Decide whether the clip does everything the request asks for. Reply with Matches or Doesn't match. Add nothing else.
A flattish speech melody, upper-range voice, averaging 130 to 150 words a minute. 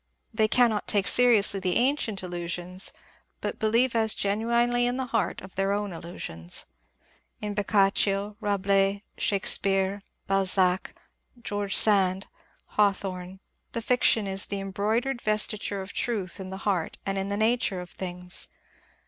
Matches